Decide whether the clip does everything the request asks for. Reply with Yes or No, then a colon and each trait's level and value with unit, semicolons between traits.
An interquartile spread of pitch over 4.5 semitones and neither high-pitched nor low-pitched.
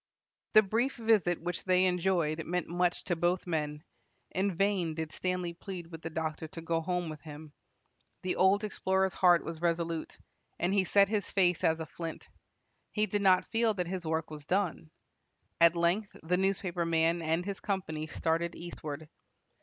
No: average, 2.7 semitones; medium, 175 Hz